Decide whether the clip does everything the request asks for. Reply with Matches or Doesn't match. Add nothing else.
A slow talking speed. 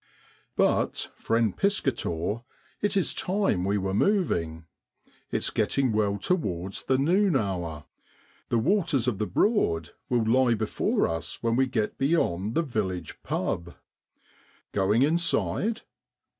Matches